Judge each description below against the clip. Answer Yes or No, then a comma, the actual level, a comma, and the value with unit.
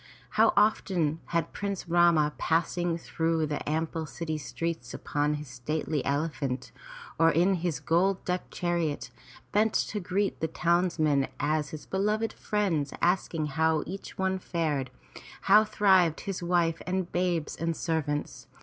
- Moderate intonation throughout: Yes, average, 3.1 semitones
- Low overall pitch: No, medium, 165 Hz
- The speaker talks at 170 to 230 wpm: No, slow, 135 wpm